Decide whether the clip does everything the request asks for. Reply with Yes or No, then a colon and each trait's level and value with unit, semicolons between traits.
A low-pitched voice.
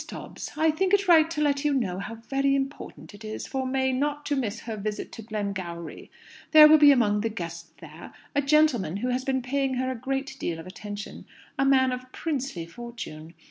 No: very high, 255 Hz